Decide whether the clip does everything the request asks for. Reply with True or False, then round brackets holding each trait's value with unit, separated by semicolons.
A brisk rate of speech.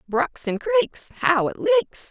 False (170 wpm)